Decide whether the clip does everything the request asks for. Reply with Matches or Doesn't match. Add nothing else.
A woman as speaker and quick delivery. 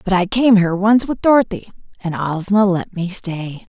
Doesn't match